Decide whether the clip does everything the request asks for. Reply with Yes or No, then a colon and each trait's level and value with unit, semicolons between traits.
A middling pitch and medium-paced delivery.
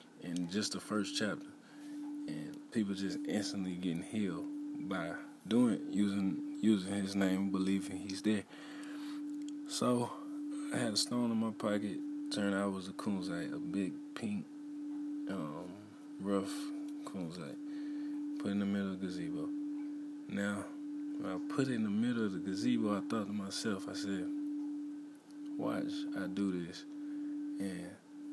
Yes: medium, 150 Hz; average, 150 wpm